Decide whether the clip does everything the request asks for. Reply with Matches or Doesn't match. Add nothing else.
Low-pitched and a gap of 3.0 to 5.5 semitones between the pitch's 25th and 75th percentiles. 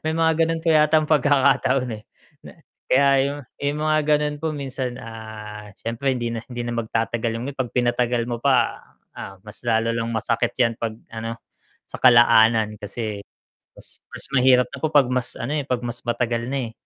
Matches